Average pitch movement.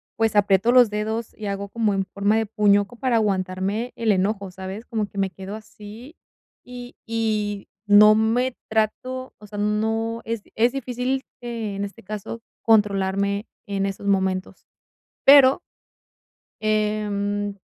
No: narrow, 2.2 semitones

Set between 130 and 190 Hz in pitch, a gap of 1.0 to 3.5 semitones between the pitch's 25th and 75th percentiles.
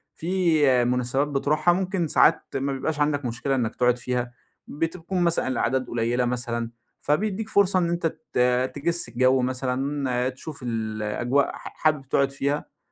No: low, 135 Hz; average, 4.4 semitones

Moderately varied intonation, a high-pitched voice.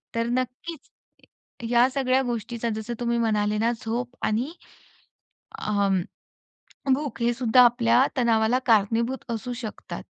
No: narrow, 2.2 semitones; high, 235 Hz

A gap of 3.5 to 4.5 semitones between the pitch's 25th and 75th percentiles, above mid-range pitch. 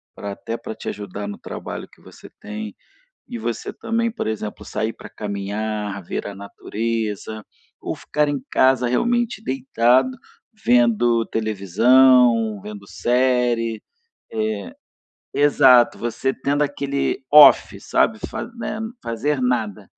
No: average, 3.8 semitones; low, 115 Hz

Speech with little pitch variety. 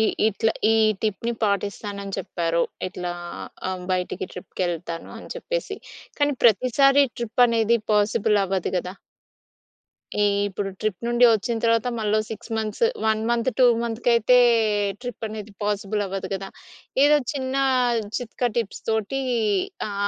No: average, 3.3 semitones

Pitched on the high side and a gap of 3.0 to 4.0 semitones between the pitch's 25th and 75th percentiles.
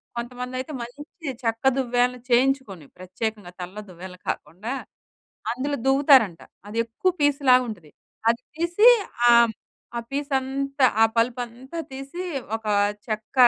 Yes: very high, 250 Hz; average, 3.6 semitones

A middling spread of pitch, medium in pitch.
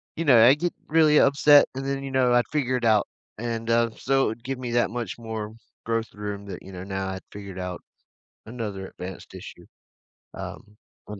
No: average, 4.4 semitones; low, 115 Hz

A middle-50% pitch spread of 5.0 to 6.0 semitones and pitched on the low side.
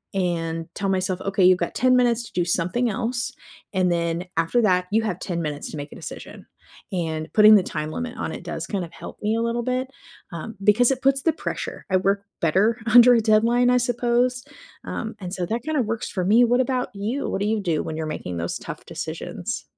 No: average, 5.3 semitones; high, 210 Hz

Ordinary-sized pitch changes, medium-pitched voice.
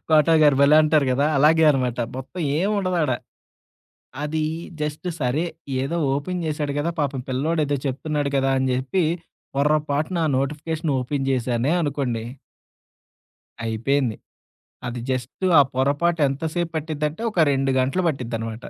Yes: average, 3.2 semitones; medium, 145 Hz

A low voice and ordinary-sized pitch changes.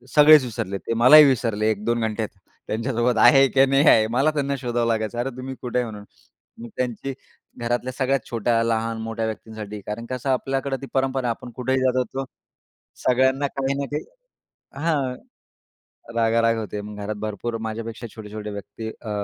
Yes: low, 120 Hz; average, 3.2 semitones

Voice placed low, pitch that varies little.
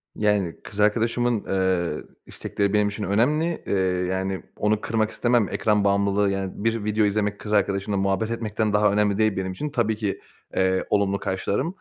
Yes: low, 105 Hz; narrow, 2.0 semitones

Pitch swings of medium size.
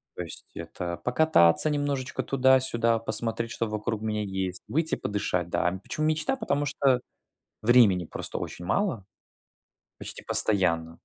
No: wide, 6.7 semitones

